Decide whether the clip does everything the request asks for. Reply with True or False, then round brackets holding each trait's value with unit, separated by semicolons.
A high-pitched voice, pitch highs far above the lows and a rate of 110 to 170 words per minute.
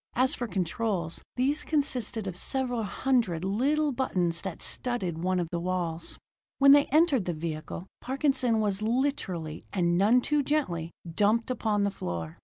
True (210 Hz; 7.1 semitones; 155 wpm)